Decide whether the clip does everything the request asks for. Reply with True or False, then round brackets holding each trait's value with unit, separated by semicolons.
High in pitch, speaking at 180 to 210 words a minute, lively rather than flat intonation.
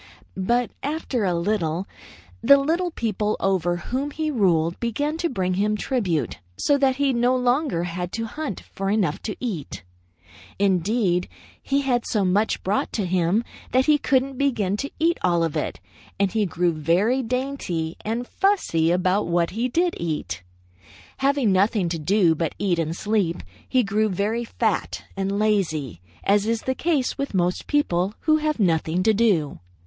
False (210 Hz; 165 wpm; 6.4 semitones)